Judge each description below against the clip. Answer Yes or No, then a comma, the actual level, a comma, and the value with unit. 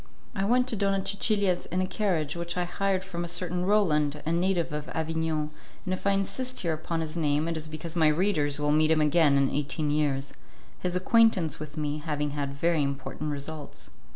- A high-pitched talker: No, medium, 160 Hz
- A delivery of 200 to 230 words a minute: Yes, fast, 205 wpm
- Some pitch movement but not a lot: Yes, average, 3.7 semitones